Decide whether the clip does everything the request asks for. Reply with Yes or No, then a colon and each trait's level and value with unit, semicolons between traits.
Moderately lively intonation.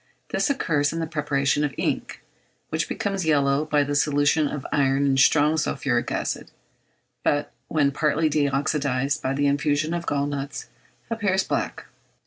No: narrow, 1.8 semitones